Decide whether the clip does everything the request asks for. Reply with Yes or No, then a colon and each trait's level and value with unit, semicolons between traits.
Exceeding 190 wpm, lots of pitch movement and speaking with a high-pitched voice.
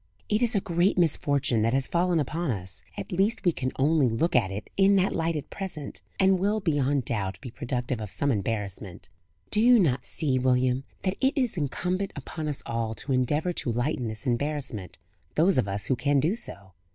No: average, 200 wpm; wide, 7.0 semitones; medium, 140 Hz